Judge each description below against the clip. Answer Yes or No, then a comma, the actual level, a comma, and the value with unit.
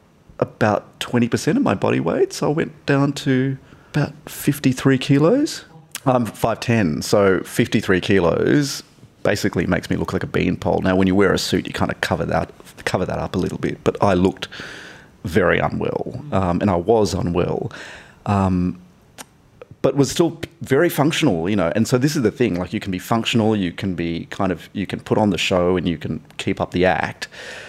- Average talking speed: Yes, average, 195 wpm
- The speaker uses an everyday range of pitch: No, wide, 6.7 semitones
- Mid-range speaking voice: No, low, 115 Hz